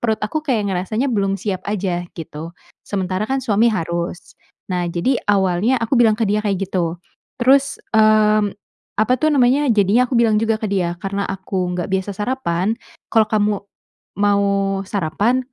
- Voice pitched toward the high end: Yes, high, 205 Hz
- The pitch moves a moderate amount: Yes, average, 3.6 semitones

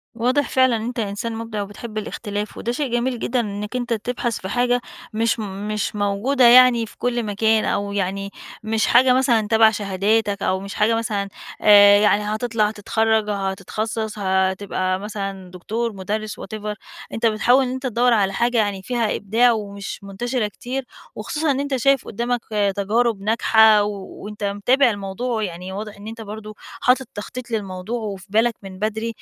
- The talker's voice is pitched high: Yes, high, 215 Hz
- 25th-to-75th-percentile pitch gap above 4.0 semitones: No, average, 2.8 semitones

